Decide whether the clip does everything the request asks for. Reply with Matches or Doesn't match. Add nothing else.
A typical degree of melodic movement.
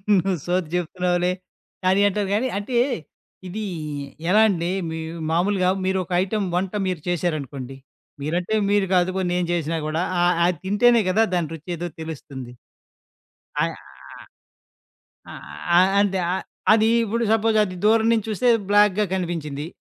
Matches